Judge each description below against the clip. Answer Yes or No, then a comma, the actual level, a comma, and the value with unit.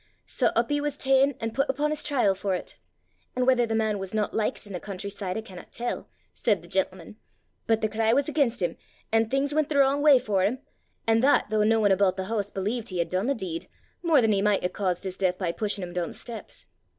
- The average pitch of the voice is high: Yes, high, 220 Hz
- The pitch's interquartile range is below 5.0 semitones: No, average, 5.3 semitones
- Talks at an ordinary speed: No, fast, 250 wpm